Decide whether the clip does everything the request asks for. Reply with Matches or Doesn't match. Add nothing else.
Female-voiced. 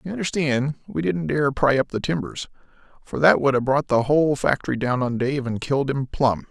Doesn't match